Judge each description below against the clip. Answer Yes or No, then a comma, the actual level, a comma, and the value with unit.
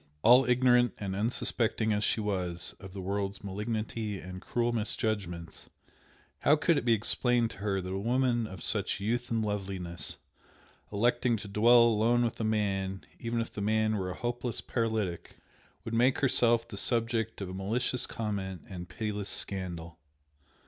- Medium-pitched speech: No, low, 110 Hz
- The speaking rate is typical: Yes, average, 160 wpm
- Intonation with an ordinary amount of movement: Yes, average, 3.4 semitones